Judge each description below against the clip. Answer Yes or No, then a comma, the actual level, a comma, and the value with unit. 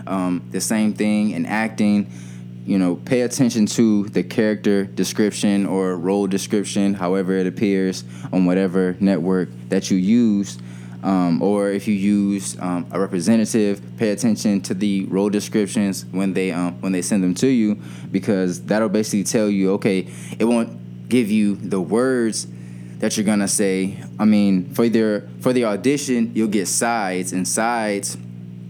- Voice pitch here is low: Yes, low, 100 Hz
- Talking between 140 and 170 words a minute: Yes, average, 160 wpm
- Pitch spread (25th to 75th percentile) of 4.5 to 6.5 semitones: No, average, 2.8 semitones